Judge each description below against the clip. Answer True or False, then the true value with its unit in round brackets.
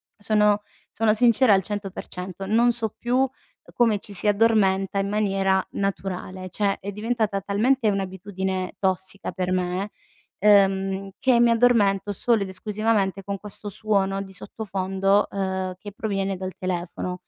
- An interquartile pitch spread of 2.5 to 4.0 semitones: False (2.0 semitones)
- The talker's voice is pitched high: True (195 Hz)